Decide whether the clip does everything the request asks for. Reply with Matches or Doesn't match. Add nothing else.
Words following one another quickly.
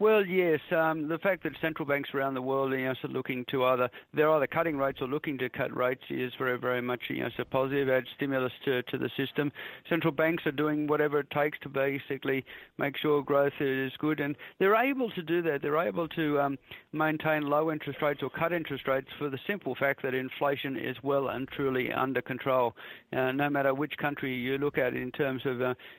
Matches